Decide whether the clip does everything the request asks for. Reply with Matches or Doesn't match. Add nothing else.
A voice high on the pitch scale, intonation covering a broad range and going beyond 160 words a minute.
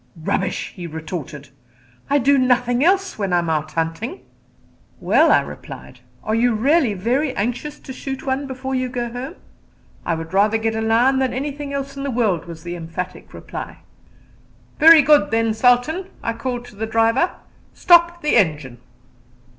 Matches